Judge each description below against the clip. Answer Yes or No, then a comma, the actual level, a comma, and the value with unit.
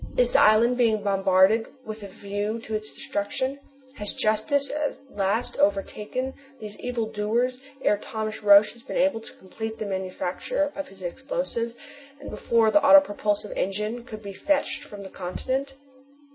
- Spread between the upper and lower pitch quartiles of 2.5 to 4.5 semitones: Yes, average, 4.2 semitones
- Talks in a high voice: Yes, high, 220 Hz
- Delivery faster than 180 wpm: No, average, 160 wpm